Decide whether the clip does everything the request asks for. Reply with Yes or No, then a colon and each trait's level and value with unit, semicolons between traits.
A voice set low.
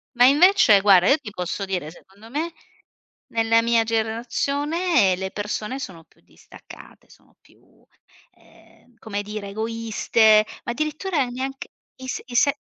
No: high, 230 Hz